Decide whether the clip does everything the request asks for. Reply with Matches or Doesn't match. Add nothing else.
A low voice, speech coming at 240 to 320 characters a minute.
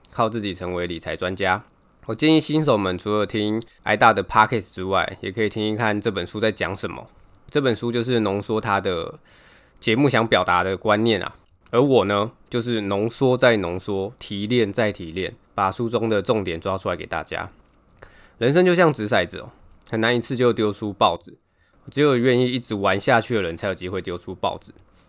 Matches